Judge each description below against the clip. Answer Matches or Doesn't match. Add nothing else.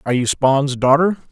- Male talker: Matches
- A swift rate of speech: Doesn't match